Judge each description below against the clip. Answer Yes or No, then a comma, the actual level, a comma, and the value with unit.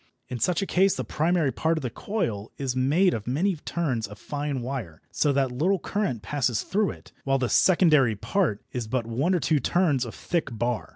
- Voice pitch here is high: No, medium, 140 Hz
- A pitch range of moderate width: No, wide, 6.1 semitones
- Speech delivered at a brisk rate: Yes, fast, 210 wpm